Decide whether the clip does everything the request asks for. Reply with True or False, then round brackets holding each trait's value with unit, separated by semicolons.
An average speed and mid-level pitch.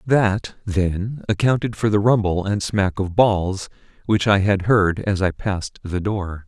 False (175 wpm; 100 Hz)